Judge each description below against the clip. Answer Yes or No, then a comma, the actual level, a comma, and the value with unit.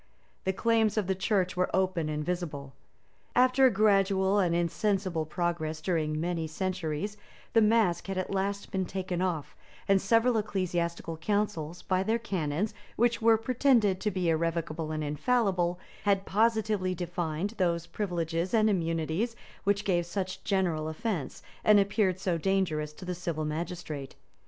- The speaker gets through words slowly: No, average, 150 wpm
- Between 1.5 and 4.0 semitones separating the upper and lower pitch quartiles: Yes, average, 3.7 semitones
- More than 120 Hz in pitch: Yes, medium, 185 Hz